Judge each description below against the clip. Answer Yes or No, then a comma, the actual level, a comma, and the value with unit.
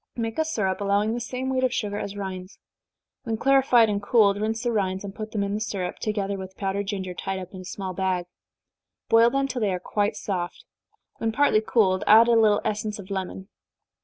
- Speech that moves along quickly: Yes, fast, 215 wpm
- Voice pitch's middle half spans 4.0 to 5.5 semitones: No, average, 2.8 semitones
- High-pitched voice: Yes, high, 205 Hz